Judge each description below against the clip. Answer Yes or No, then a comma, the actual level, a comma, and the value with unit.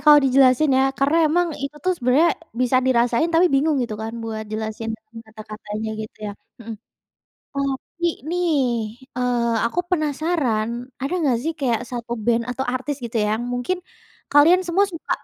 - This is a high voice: Yes, very high, 255 Hz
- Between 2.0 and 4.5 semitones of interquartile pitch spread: No, average, 5.0 semitones